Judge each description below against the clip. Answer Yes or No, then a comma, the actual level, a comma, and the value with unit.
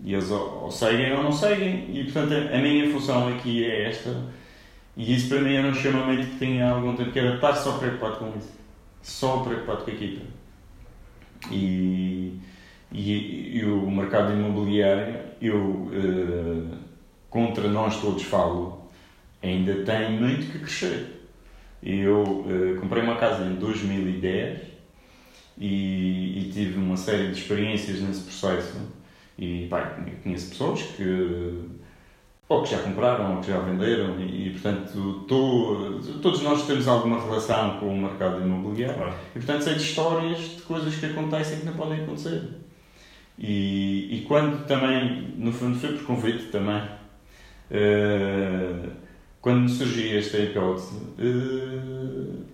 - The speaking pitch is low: Yes, low, 105 Hz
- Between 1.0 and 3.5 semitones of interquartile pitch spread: No, average, 5.0 semitones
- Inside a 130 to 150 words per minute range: Yes, average, 145 wpm